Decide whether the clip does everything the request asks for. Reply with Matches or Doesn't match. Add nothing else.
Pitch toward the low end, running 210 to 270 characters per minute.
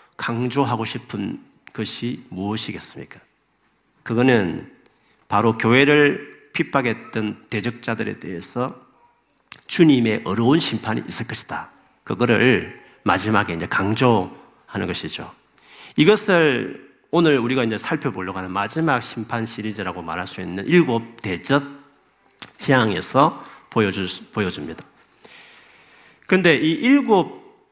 Matches